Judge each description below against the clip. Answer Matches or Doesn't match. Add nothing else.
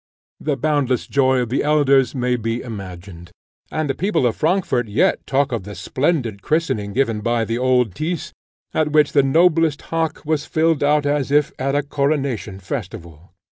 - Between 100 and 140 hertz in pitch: Matches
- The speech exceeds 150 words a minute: Matches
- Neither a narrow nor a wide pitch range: Matches